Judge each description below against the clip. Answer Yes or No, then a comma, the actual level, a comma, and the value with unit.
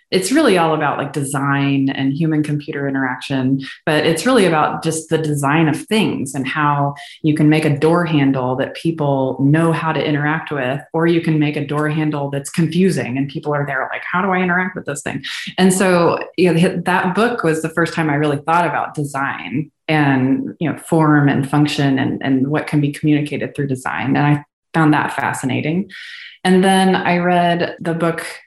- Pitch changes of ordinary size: Yes, average, 3.0 semitones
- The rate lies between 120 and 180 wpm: No, average, 200 wpm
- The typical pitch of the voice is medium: Yes, medium, 150 Hz